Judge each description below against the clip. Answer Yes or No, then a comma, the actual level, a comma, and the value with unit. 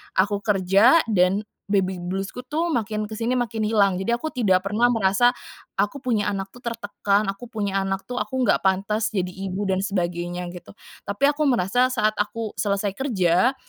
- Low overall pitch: No, high, 205 Hz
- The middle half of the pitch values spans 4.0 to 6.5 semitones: No, average, 3.5 semitones